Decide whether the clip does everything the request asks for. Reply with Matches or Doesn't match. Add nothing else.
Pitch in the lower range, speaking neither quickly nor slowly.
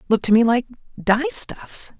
Doesn't match